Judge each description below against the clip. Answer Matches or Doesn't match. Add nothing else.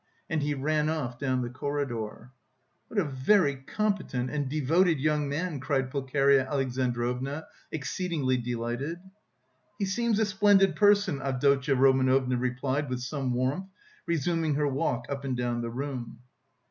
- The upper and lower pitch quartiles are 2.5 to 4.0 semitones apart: Matches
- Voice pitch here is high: Doesn't match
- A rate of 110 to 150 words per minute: Matches